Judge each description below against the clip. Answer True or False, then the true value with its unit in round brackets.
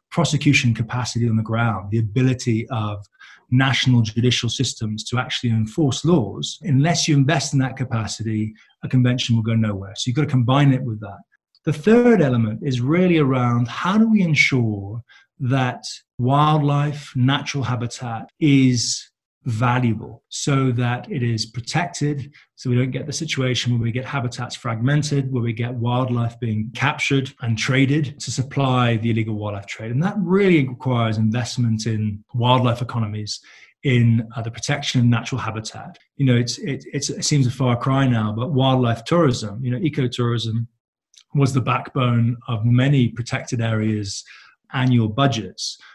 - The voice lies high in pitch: False (125 Hz)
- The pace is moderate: True (160 wpm)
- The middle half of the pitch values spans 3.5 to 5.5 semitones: False (3.1 semitones)